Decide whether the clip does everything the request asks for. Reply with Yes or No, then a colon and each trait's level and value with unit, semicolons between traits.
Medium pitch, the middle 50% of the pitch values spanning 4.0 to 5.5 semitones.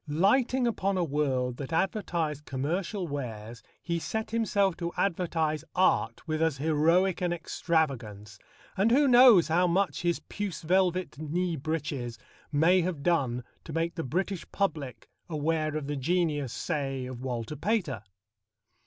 Yes: medium, 165 Hz; average, 4.6 semitones